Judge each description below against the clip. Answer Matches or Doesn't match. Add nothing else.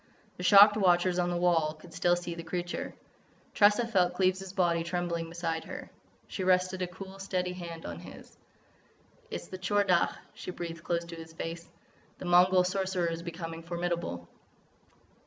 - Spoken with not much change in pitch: Matches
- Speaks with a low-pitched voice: Doesn't match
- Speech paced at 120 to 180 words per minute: Matches